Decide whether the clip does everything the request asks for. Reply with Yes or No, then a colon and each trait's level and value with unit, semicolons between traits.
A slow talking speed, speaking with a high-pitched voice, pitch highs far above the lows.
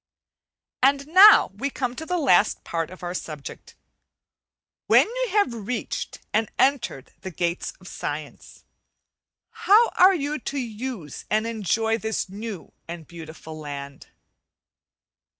Yes: slow, 130 wpm; high, 220 Hz; wide, 8.4 semitones